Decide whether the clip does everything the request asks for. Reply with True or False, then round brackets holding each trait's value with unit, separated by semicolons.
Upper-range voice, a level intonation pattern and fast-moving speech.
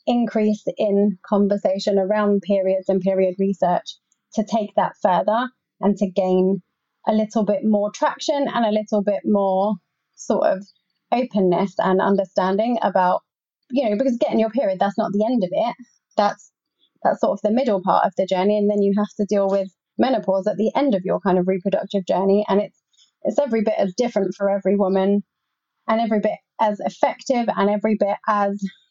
False (205 Hz; 2.3 semitones; 185 wpm)